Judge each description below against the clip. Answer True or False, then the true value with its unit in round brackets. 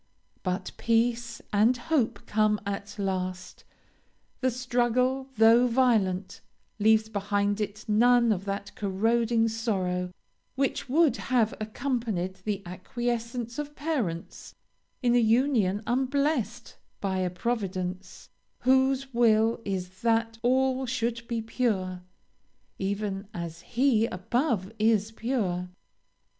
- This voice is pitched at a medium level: False (225 Hz)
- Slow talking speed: True (110 wpm)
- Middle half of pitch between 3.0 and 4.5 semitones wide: True (3.7 semitones)